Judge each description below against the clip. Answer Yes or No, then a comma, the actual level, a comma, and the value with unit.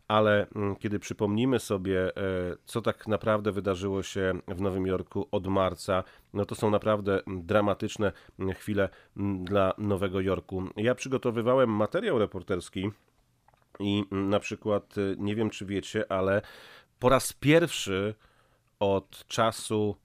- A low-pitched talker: Yes, low, 100 Hz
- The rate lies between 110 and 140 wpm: Yes, average, 120 wpm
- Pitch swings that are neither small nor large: No, narrow, 2.0 semitones